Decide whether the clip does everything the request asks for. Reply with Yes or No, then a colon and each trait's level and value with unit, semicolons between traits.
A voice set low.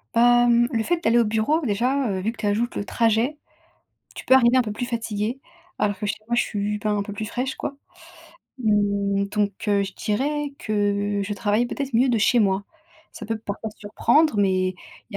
No: high, 220 Hz